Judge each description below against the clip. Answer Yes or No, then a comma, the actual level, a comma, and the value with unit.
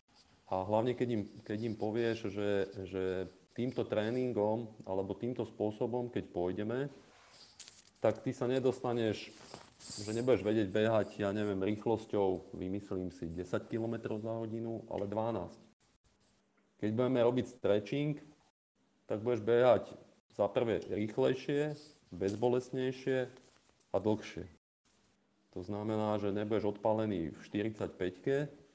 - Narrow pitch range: No, average, 3.4 semitones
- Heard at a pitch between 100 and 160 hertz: Yes, low, 110 Hz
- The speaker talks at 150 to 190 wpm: No, average, 115 wpm